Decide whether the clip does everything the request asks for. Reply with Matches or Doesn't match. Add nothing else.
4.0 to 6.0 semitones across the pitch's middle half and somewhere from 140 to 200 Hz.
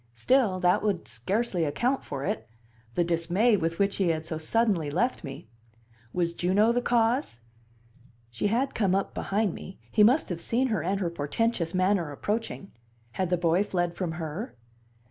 Matches